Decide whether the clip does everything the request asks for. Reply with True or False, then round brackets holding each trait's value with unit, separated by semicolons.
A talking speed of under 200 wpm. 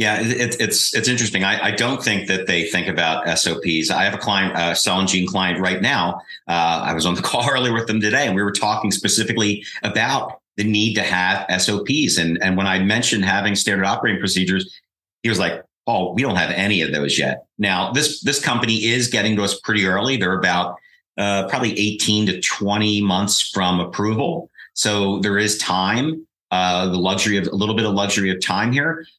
False (205 wpm)